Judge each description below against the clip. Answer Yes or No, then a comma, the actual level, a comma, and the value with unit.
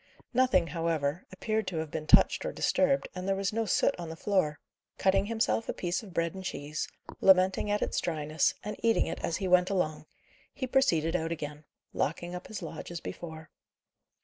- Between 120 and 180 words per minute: No, average, 195 wpm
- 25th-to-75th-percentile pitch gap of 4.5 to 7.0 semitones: No, average, 3.9 semitones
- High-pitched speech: No, medium, 180 Hz